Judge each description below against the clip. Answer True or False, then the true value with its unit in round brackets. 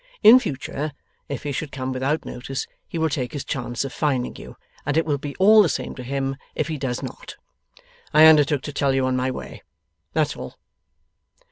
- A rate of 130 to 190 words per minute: False (205 wpm)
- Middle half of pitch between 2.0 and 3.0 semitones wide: True (2.7 semitones)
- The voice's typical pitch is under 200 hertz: True (140 Hz)